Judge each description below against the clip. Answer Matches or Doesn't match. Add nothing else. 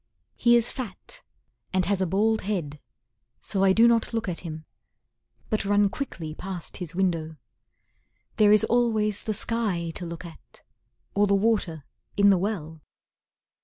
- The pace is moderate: Matches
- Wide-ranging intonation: Doesn't match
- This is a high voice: Matches